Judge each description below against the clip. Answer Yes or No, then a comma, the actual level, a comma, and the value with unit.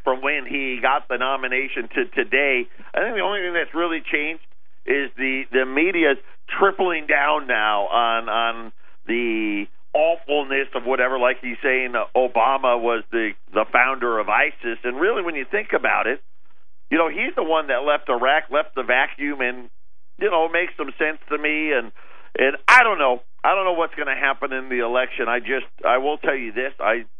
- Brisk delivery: No, average, 195 wpm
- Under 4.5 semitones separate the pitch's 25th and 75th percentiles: Yes, average, 4.1 semitones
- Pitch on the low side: Yes, low, 130 Hz